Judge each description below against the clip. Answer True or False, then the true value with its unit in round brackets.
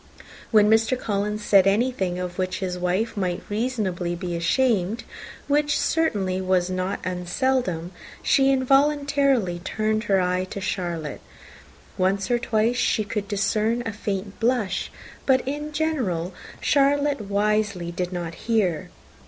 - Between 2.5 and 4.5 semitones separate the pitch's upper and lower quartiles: False (5.1 semitones)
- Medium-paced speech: False (130 wpm)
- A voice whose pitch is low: False (205 Hz)